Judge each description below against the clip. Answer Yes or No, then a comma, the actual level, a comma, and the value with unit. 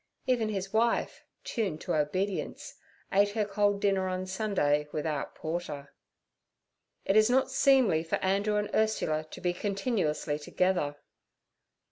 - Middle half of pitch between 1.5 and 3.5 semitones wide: No, average, 5.1 semitones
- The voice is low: No, high, 195 Hz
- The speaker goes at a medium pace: No, slow, 120 wpm